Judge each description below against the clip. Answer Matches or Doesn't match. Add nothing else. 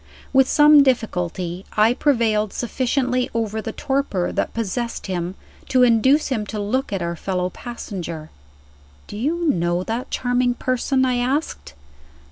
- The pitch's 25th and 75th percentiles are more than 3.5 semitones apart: Matches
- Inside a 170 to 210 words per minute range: Doesn't match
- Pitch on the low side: Doesn't match